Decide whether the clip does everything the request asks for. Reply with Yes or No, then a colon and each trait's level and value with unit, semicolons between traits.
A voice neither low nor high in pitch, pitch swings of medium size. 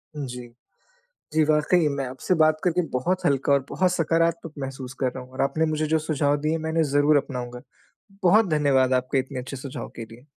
Yes: medium, 145 Hz; average, 3.5 semitones